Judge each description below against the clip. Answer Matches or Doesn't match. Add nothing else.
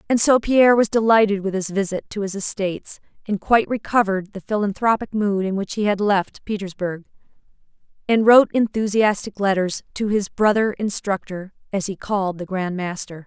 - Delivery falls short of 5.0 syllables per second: Doesn't match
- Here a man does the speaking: Doesn't match